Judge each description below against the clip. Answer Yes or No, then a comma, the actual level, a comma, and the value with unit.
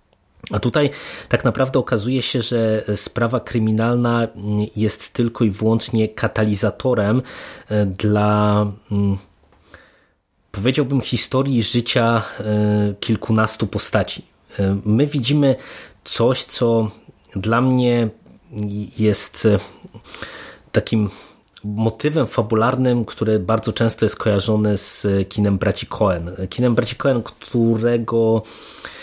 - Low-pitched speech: Yes, low, 110 Hz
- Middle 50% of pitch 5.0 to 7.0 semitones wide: No, narrow, 2.4 semitones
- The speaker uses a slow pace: Yes, slow, 90 wpm